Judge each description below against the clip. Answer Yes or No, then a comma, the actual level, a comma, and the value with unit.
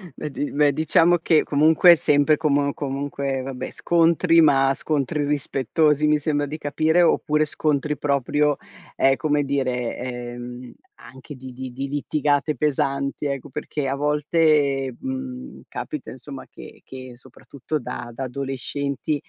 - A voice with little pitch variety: Yes, narrow, 2.1 semitones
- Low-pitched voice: No, medium, 145 Hz